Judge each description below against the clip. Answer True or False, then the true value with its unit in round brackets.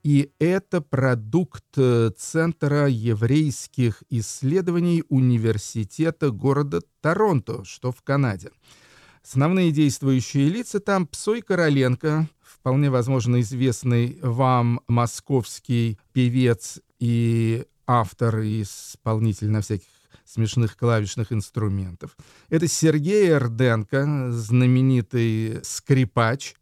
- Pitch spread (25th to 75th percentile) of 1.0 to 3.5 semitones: False (4.1 semitones)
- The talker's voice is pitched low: True (125 Hz)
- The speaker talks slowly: True (85 wpm)